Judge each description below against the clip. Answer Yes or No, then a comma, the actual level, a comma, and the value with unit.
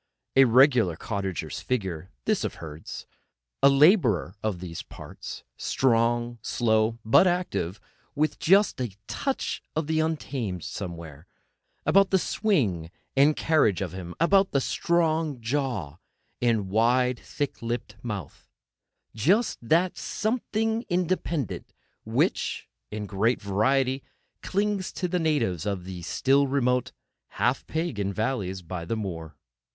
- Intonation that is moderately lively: No, wide, 8.4 semitones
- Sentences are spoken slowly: Yes, slow, 120 wpm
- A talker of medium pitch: No, low, 120 Hz